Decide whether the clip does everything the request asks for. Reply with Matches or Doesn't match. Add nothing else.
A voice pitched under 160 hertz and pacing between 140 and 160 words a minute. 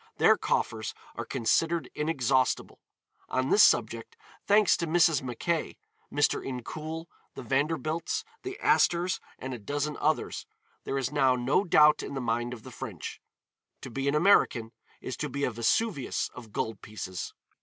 Matches